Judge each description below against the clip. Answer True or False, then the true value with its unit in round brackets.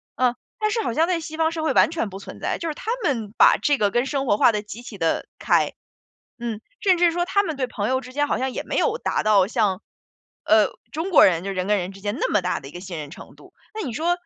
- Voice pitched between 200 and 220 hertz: False (245 Hz)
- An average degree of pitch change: False (7.9 semitones)